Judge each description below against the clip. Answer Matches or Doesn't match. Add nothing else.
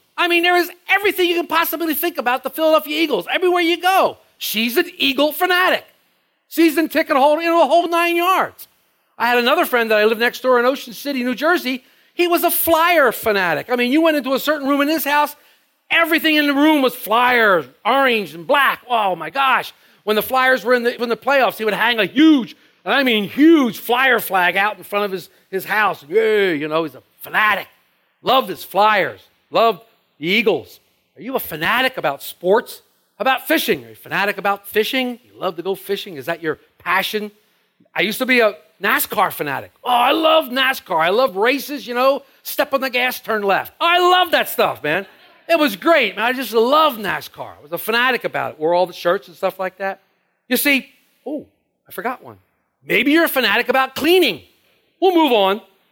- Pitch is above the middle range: Matches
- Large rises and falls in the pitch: Matches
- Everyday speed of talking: Doesn't match